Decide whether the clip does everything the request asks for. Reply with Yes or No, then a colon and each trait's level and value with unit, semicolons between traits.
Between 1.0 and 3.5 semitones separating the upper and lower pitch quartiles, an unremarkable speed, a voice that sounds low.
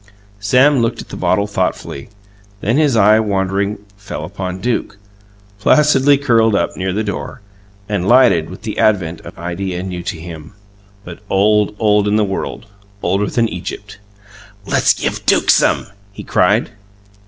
Yes: average, 3.0 semitones; average, 155 wpm; low, 100 Hz